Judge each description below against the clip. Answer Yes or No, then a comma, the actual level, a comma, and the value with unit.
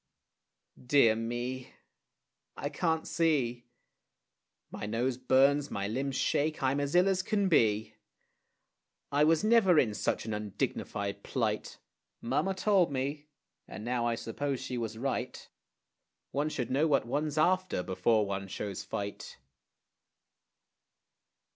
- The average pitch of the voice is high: No, low, 130 Hz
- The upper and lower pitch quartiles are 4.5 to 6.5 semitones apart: Yes, average, 5.2 semitones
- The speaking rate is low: Yes, slow, 125 wpm